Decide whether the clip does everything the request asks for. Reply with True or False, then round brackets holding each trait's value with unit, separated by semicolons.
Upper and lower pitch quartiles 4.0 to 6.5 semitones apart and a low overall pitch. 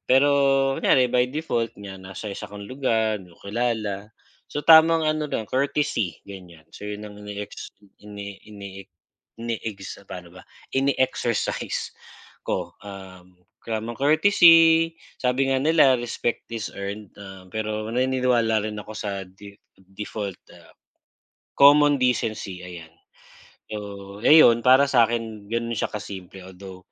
True (4.5 semitones; 110 Hz)